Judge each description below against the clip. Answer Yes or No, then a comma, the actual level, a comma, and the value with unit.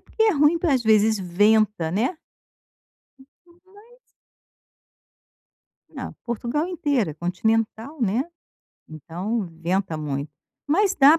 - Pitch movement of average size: No, wide, 8.2 semitones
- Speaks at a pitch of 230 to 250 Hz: No, high, 220 Hz